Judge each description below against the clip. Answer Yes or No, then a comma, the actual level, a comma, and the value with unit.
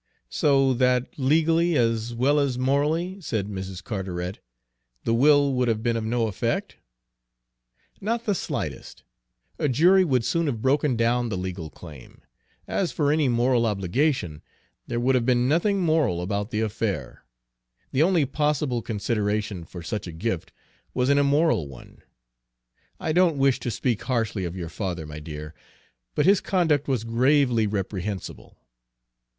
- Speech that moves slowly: No, average, 150 wpm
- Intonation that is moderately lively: No, wide, 6.2 semitones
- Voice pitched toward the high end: No, low, 120 Hz